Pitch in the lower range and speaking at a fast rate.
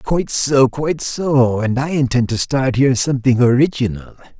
No: low, 130 Hz; average, 165 wpm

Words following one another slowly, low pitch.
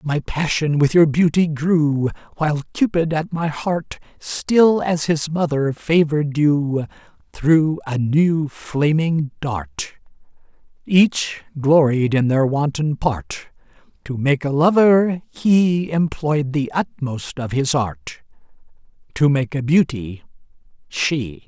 No: slow, 125 wpm; medium, 150 Hz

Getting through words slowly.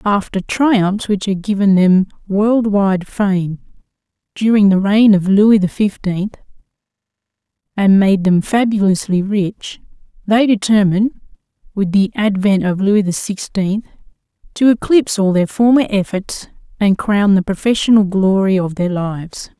Yes: slow, 130 wpm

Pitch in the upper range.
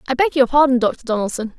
Yes: very high, 255 Hz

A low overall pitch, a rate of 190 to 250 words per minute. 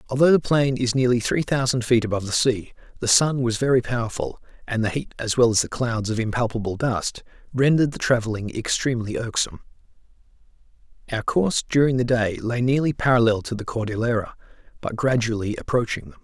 No: low, 120 Hz; average, 175 wpm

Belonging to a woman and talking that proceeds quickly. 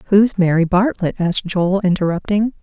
No: female; slow, 135 wpm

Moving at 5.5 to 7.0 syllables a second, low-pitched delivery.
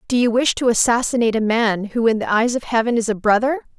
No: 6.4 syllables/s; high, 230 Hz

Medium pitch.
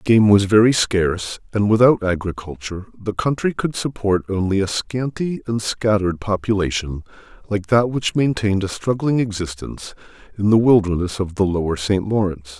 No: low, 105 Hz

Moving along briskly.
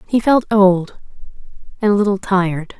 No: average, 150 wpm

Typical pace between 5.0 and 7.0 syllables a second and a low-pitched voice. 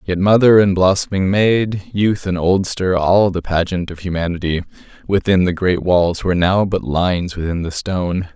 No: 4.8 syllables/s; very low, 90 Hz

